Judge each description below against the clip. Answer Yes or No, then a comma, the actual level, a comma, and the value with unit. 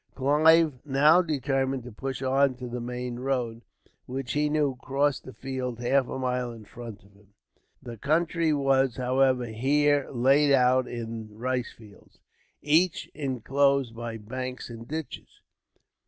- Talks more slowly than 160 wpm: Yes, average, 145 wpm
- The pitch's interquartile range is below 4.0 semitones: Yes, narrow, 2.6 semitones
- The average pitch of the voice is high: No, low, 130 Hz